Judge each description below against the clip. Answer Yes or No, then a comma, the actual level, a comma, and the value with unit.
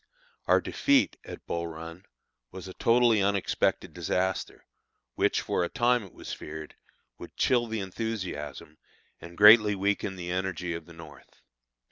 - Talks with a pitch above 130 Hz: No, very low, 95 Hz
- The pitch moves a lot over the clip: No, average, 4.2 semitones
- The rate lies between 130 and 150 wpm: Yes, average, 145 wpm